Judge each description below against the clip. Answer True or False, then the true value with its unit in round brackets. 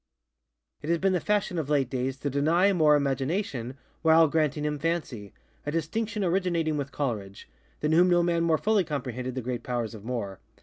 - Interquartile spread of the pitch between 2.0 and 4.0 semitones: False (4.9 semitones)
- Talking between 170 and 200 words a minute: True (175 wpm)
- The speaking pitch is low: False (150 Hz)